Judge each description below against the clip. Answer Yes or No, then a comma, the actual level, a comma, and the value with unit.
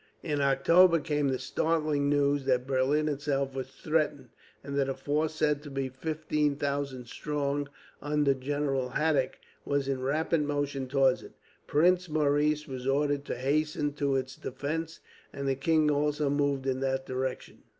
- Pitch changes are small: Yes, narrow, 1.8 semitones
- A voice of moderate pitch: Yes, medium, 145 Hz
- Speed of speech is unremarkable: Yes, average, 160 wpm